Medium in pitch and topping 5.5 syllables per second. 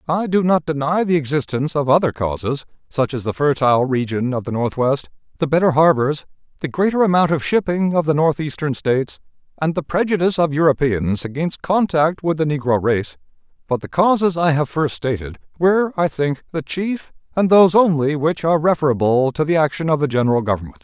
Yes: medium, 150 Hz; 5.7 syllables/s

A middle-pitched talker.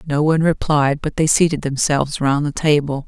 Yes: medium, 150 Hz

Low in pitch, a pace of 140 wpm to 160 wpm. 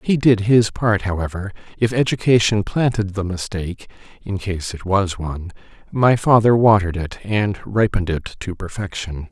Yes: low, 100 Hz; average, 150 wpm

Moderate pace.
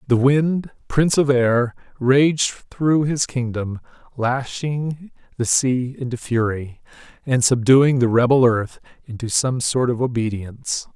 No: slow, 130 wpm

